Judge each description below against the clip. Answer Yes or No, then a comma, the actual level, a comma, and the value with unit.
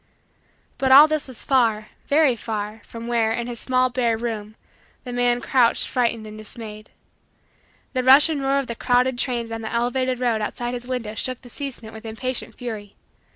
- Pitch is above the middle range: Yes, high, 240 Hz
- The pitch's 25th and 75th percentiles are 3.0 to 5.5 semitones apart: No, narrow, 2.4 semitones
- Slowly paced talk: No, average, 185 wpm